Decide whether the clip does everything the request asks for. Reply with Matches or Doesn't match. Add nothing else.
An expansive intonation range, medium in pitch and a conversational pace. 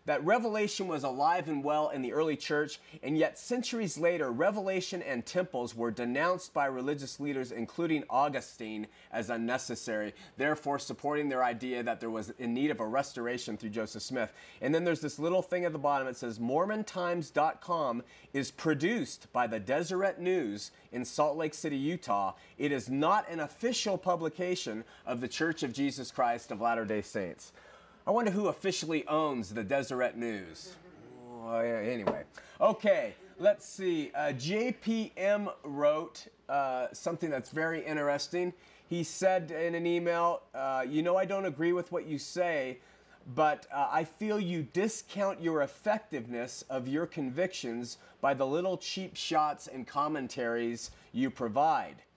Matches